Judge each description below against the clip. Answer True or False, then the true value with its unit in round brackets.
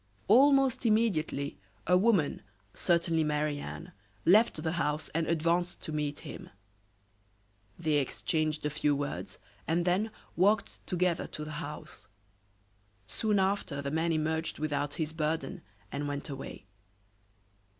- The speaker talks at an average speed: False (130 wpm)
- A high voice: False (160 Hz)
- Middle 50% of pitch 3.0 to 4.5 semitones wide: True (3.3 semitones)